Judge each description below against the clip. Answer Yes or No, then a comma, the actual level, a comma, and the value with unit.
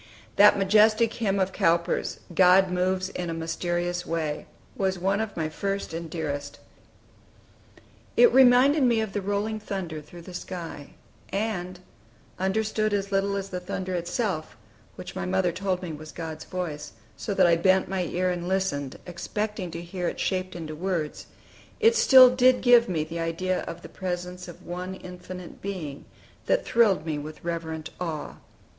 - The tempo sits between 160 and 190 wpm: Yes, average, 165 wpm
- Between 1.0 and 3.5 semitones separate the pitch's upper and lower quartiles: Yes, average, 3.0 semitones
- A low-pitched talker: No, medium, 185 Hz